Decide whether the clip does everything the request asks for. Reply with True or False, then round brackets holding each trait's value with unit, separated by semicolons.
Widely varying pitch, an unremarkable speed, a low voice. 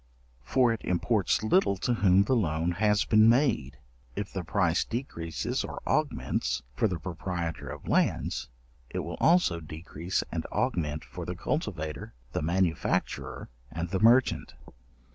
False (4.8 semitones; 145 wpm; 90 Hz)